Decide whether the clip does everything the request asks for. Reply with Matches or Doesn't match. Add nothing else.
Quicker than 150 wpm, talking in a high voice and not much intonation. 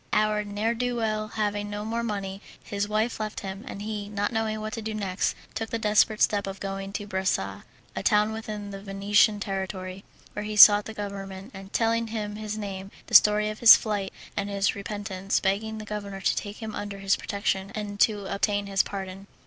Matches